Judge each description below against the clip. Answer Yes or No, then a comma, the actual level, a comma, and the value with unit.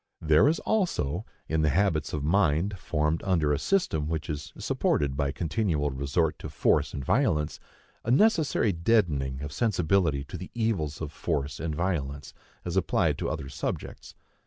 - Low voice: Yes, very low, 80 Hz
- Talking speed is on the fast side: No, average, 160 wpm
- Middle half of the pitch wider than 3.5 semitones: Yes, average, 4.9 semitones